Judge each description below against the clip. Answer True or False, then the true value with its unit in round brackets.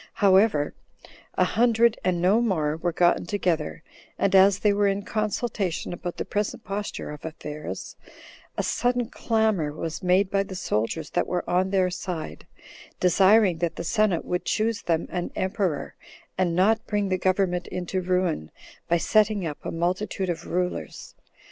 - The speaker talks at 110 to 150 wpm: False (160 wpm)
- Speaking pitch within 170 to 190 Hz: True (185 Hz)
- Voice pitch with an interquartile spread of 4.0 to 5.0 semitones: False (3.0 semitones)